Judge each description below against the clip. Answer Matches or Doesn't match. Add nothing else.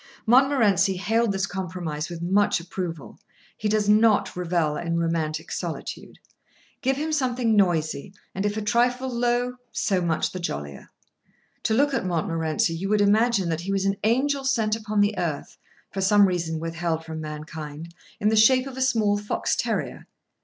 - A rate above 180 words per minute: Doesn't match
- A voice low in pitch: Doesn't match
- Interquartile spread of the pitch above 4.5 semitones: Matches